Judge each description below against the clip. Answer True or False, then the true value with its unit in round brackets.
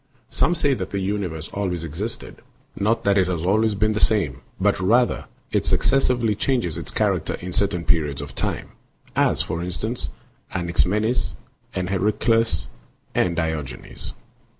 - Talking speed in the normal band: True (155 wpm)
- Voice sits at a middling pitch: False (95 Hz)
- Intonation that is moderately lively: True (4.3 semitones)